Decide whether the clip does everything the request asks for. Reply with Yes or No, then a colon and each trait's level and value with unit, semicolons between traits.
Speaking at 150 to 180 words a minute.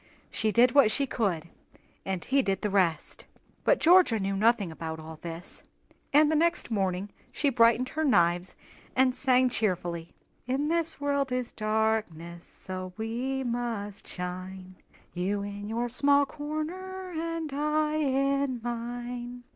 No: average, 140 wpm